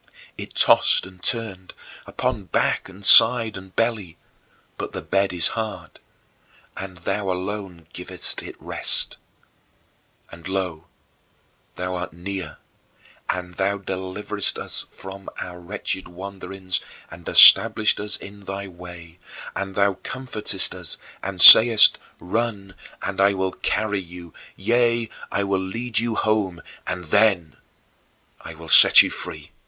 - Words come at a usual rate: No, slow, 130 wpm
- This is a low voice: Yes, very low, 95 Hz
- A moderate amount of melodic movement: No, narrow, 2.3 semitones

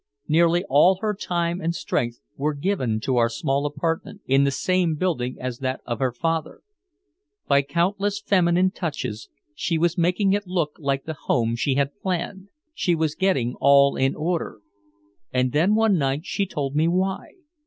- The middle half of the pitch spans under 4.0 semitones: No, average, 4.9 semitones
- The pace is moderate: Yes, average, 170 wpm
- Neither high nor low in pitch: Yes, medium, 160 Hz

